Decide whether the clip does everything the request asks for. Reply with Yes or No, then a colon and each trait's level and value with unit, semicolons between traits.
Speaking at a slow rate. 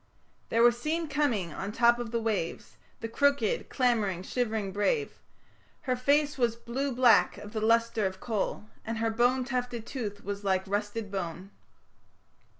No: average, 160 wpm